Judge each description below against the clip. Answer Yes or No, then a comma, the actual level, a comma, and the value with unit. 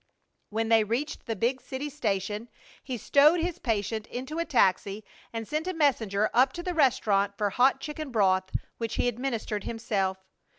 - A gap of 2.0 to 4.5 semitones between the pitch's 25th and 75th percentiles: No, average, 5.1 semitones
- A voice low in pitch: No, high, 230 Hz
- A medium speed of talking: Yes, average, 170 wpm